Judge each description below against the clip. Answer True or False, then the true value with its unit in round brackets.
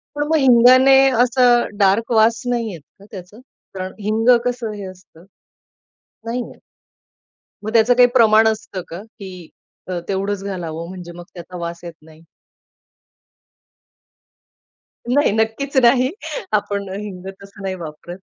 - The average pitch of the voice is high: True (205 Hz)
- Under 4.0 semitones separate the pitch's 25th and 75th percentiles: False (4.3 semitones)